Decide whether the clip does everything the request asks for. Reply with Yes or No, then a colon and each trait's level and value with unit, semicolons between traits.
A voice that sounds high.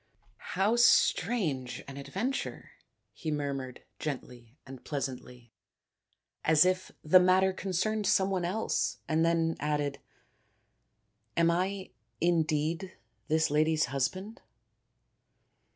No: medium, 160 Hz